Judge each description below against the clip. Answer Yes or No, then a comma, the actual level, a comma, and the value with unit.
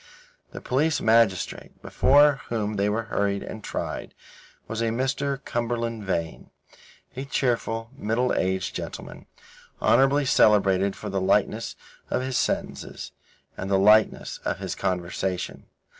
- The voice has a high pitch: No, low, 110 Hz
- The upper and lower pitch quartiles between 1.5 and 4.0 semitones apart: No, average, 4.5 semitones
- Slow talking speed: Yes, slow, 130 wpm